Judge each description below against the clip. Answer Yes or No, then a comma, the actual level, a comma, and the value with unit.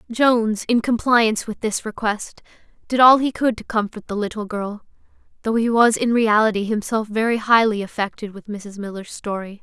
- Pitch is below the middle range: No, high, 220 Hz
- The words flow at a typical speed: Yes, average, 175 wpm